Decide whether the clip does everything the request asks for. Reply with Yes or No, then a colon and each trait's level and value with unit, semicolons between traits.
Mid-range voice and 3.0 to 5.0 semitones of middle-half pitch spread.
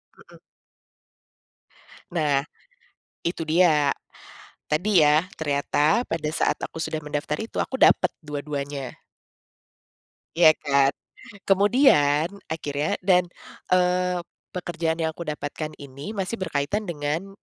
Yes: medium, 155 Hz; average, 3.7 semitones